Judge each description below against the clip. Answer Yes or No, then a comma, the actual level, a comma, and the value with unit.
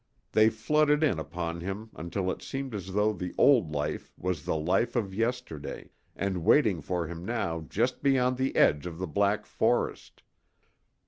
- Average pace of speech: Yes, average, 170 wpm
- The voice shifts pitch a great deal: Yes, wide, 6.0 semitones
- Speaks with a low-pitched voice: Yes, very low, 95 Hz